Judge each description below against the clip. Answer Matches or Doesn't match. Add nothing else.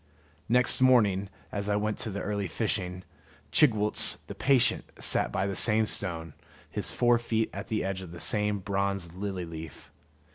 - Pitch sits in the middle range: Doesn't match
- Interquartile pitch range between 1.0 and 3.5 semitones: Matches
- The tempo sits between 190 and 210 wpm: Doesn't match